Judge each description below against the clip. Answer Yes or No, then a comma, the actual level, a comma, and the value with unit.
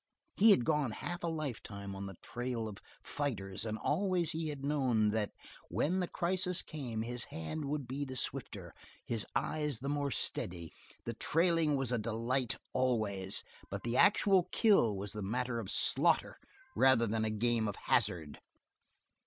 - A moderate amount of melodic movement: No, wide, 5.7 semitones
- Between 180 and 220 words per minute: No, average, 165 wpm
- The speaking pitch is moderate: No, low, 125 Hz